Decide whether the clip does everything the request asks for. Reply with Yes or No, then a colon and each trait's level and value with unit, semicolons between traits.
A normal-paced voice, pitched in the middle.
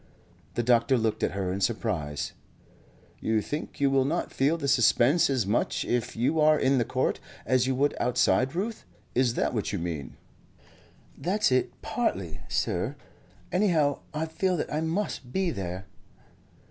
No: average, 160 wpm; low, 130 Hz